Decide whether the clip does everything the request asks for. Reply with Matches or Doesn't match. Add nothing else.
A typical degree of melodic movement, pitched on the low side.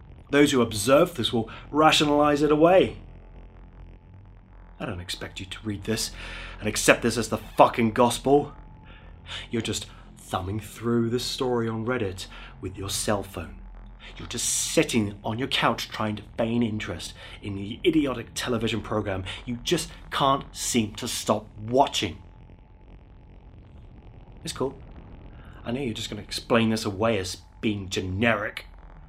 Matches